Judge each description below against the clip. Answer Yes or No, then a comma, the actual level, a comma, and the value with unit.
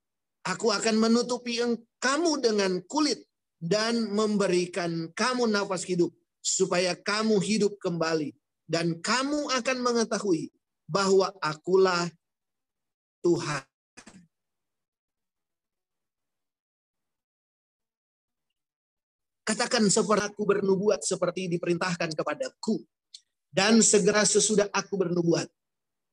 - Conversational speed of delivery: No, slow, 80 wpm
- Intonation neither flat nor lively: Yes, average, 4.2 semitones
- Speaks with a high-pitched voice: Yes, high, 195 Hz